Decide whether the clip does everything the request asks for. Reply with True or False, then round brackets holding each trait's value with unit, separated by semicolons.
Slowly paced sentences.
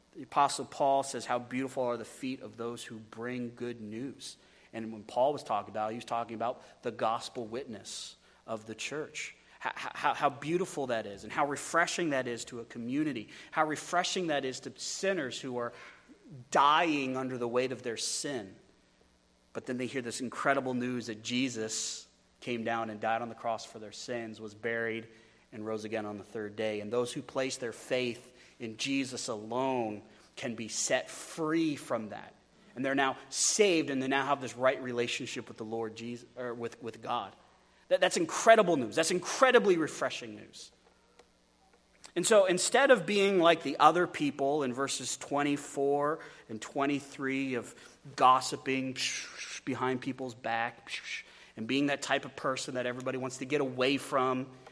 False (180 wpm)